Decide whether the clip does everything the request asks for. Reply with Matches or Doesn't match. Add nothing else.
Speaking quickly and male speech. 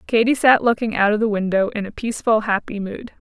Doesn't match